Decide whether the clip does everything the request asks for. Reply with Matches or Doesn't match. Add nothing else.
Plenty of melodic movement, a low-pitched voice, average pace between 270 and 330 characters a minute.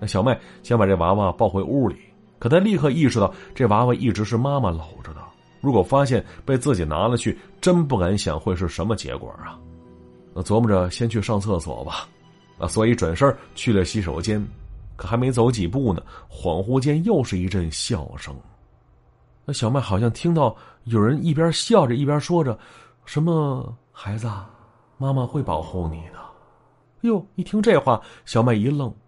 Doesn't match